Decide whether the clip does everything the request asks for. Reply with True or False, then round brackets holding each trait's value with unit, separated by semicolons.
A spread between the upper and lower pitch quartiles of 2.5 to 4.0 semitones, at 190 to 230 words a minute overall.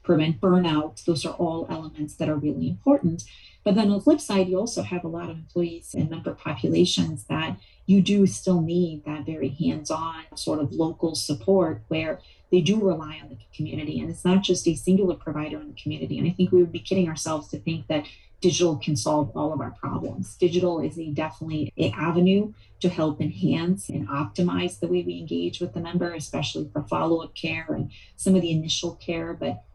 True (2.8 semitones; 205 wpm)